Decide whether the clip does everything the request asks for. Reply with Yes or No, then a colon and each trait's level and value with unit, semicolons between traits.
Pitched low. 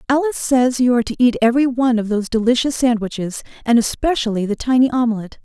No: high, 240 Hz